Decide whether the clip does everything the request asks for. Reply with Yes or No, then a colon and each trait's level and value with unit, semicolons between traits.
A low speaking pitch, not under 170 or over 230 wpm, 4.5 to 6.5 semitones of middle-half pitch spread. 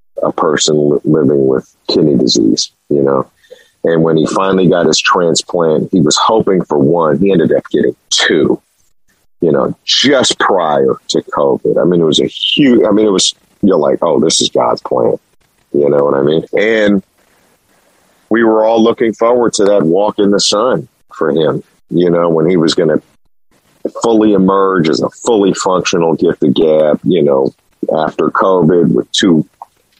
Yes: very low, 90 Hz; average, 175 wpm; wide, 5.6 semitones